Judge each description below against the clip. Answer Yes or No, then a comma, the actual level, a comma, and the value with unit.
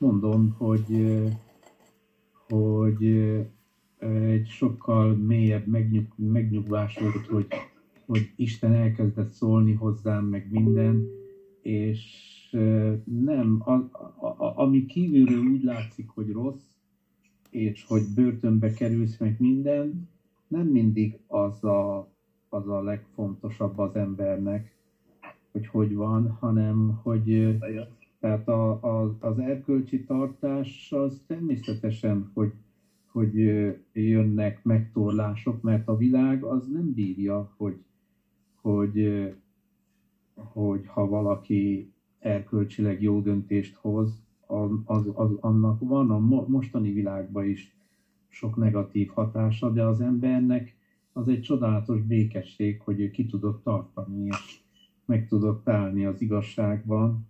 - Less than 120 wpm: Yes, average, 110 wpm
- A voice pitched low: Yes, low, 110 Hz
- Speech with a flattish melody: Yes, narrow, 2.0 semitones